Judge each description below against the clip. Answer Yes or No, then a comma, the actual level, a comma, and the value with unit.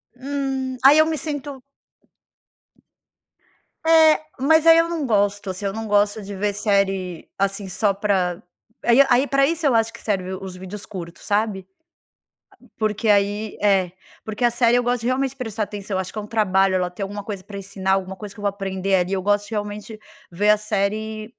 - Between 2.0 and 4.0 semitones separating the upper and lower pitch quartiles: Yes, average, 3.7 semitones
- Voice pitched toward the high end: Yes, high, 210 Hz